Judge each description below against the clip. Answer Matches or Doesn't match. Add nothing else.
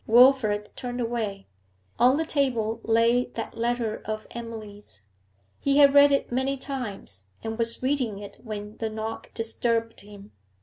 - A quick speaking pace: Doesn't match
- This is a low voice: Doesn't match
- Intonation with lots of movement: Doesn't match